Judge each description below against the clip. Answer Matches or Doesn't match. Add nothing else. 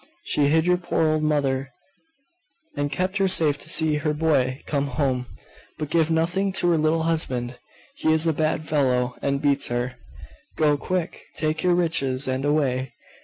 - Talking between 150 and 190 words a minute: Matches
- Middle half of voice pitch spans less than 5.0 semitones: Matches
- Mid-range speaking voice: Matches